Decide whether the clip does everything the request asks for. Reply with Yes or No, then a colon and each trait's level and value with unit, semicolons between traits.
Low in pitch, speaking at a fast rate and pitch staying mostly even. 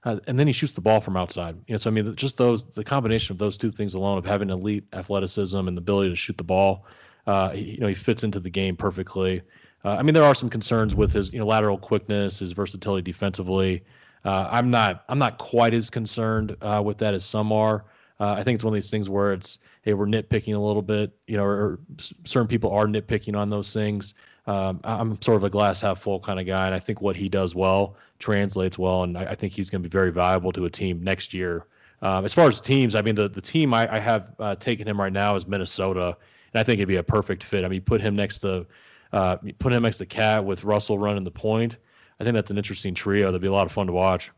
Yes: low, 105 Hz; fast, 265 wpm; narrow, 2.3 semitones